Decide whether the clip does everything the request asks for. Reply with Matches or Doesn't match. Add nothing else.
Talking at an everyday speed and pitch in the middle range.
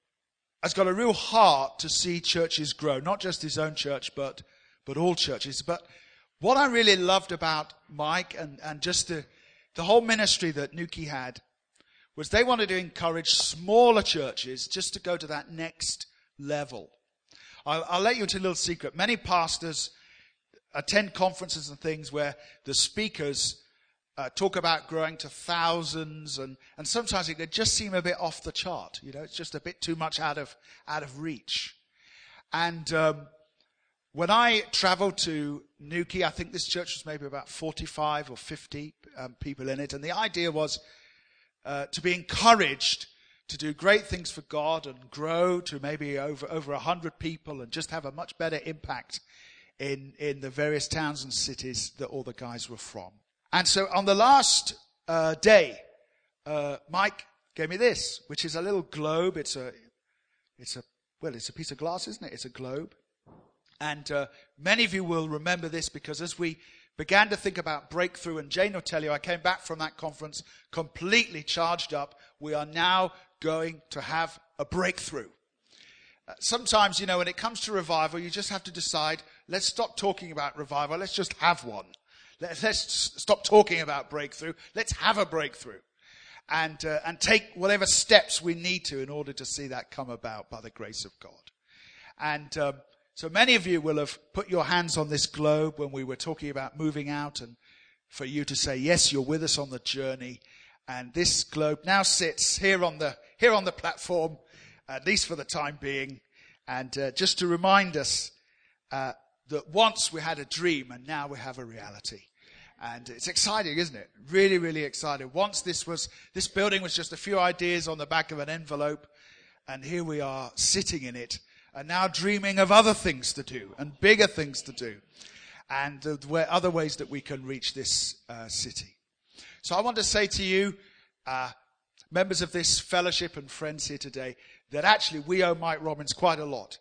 Matches